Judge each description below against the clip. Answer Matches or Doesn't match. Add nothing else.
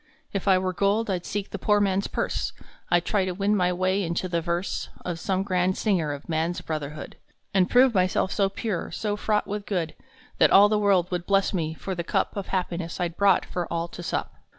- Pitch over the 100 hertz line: Matches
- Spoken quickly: Matches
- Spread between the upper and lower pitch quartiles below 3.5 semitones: Matches